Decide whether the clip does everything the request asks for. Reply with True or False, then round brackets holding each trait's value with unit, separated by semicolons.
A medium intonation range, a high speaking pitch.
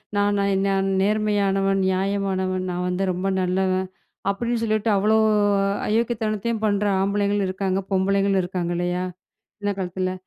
False (1.6 semitones; 195 Hz)